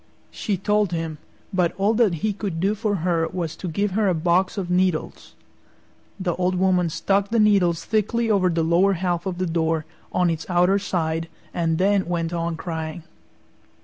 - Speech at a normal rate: Yes, average, 180 wpm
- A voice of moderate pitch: Yes, medium, 180 Hz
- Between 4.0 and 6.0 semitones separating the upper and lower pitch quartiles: No, average, 3.0 semitones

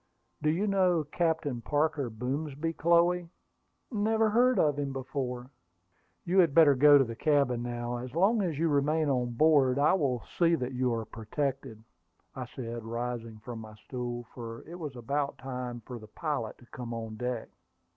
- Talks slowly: No, average, 175 wpm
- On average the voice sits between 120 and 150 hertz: Yes, low, 135 Hz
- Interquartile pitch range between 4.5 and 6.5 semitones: Yes, average, 4.8 semitones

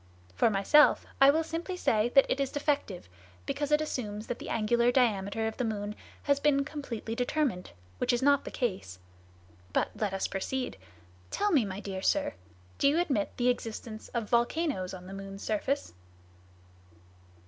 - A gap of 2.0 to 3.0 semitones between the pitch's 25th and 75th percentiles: No, wide, 5.6 semitones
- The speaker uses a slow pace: No, average, 170 wpm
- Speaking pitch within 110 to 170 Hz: No, high, 240 Hz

